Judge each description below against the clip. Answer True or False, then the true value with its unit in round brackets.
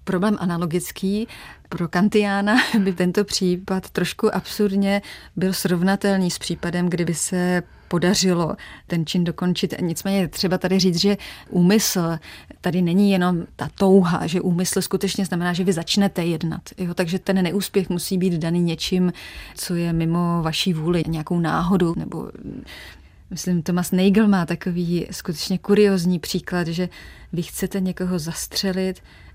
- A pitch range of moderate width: False (1.9 semitones)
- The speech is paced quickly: False (140 wpm)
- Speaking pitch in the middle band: True (180 Hz)